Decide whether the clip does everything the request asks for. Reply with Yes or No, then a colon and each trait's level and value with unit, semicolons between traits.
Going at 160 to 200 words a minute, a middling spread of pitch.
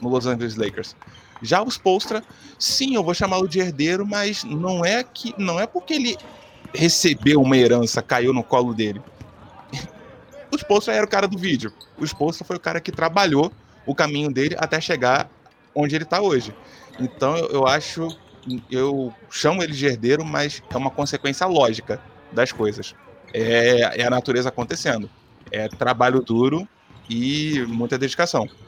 No: average, 165 wpm; wide, 6.5 semitones